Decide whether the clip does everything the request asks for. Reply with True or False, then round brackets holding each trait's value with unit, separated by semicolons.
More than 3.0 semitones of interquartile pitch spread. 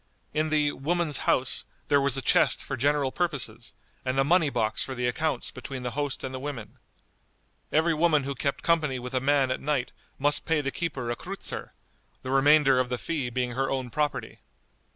False (2.7 semitones)